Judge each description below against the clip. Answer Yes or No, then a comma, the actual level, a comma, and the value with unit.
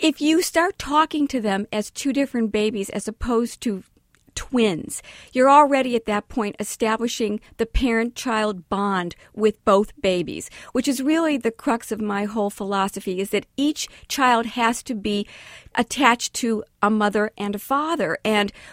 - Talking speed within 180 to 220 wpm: No, average, 165 wpm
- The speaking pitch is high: Yes, high, 225 Hz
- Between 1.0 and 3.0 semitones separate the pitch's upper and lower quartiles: No, average, 3.7 semitones